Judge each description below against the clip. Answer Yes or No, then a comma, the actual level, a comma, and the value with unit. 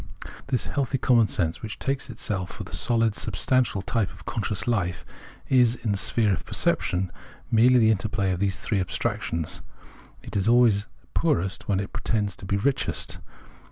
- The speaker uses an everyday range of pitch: Yes, average, 3.9 semitones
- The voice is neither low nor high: No, low, 110 Hz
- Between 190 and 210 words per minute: No, average, 160 wpm